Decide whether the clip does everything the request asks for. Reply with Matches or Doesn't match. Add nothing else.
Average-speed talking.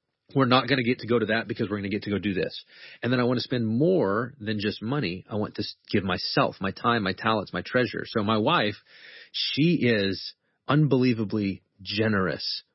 Doesn't match